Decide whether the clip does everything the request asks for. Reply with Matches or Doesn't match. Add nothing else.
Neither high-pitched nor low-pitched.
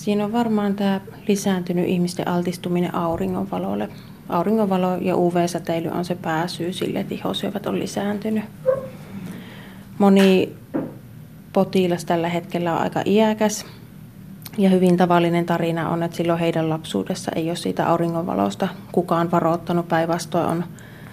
Matches